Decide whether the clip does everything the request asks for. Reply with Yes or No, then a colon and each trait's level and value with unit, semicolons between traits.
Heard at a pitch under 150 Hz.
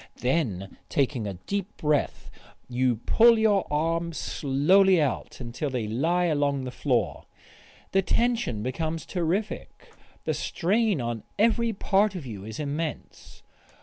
No: medium, 155 Hz